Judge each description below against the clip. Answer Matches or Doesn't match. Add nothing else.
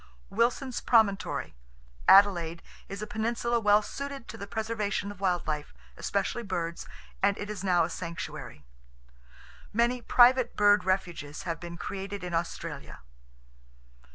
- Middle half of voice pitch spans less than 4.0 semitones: Doesn't match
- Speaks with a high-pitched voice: Matches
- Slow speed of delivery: Matches